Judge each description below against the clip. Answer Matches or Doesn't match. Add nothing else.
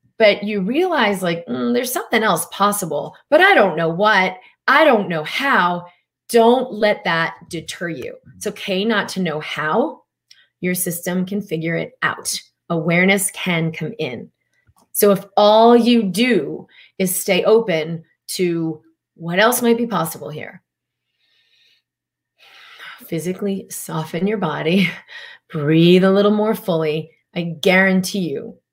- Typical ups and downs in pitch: Matches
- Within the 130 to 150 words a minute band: Matches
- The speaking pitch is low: Doesn't match